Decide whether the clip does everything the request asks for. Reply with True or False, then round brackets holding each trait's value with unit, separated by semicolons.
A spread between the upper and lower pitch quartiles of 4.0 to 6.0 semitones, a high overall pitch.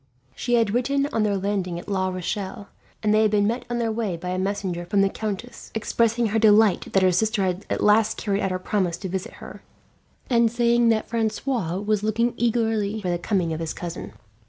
False (3.2 semitones; 210 Hz)